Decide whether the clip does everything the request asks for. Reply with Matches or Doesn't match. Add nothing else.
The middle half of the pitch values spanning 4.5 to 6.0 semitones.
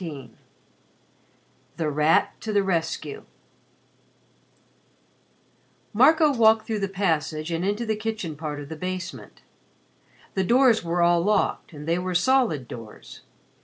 Matches